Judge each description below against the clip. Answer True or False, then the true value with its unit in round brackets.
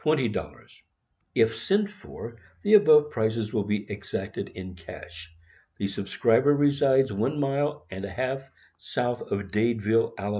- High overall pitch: False (115 Hz)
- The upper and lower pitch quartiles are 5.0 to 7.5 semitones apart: True (5.5 semitones)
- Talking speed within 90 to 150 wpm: True (140 wpm)